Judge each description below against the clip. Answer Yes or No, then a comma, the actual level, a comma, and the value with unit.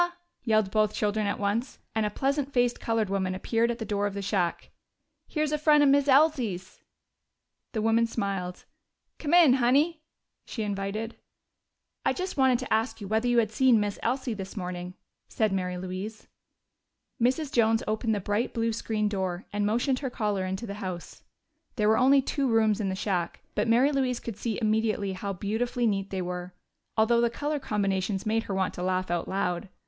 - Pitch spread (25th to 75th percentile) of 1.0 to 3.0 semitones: No, average, 3.7 semitones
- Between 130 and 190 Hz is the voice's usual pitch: No, high, 220 Hz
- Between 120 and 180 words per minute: No, average, 190 wpm